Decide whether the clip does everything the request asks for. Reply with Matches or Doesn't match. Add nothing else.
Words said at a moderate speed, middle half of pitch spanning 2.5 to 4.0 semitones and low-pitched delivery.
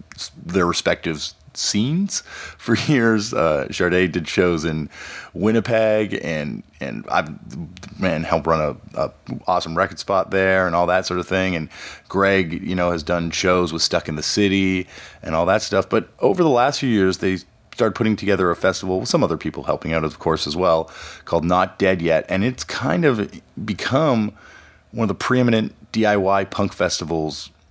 Matches